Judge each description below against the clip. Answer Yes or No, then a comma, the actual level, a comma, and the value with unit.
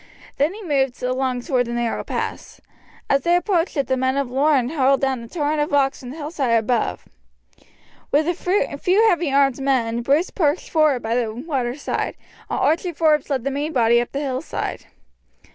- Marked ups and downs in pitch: No, average, 3.7 semitones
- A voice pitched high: Yes, very high, 275 Hz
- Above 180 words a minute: Yes, average, 190 wpm